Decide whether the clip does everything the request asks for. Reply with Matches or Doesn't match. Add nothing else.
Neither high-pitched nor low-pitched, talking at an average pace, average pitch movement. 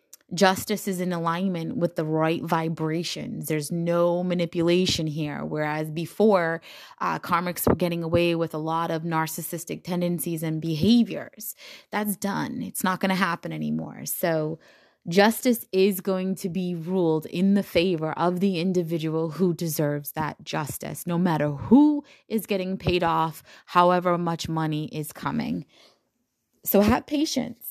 Matches